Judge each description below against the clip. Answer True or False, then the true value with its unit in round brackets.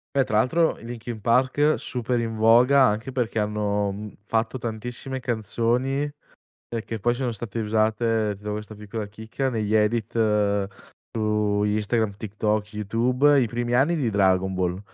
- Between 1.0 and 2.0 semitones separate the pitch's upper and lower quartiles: False (2.5 semitones)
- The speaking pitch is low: True (110 Hz)